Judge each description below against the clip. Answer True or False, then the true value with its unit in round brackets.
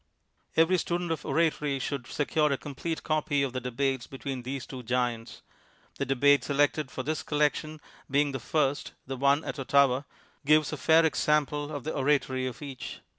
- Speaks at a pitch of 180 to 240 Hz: False (140 Hz)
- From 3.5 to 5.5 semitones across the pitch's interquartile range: False (2.5 semitones)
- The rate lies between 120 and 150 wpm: False (175 wpm)